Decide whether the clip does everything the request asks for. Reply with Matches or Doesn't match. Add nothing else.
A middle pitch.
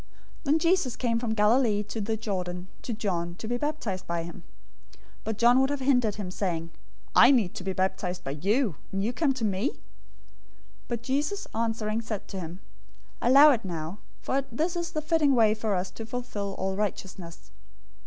Doesn't match